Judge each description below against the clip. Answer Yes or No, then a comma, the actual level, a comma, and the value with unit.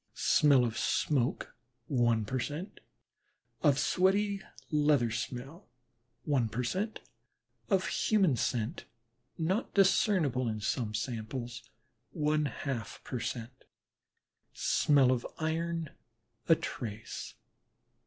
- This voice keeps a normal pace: No, slow, 105 wpm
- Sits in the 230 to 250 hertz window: No, medium, 140 Hz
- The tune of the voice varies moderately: No, wide, 5.7 semitones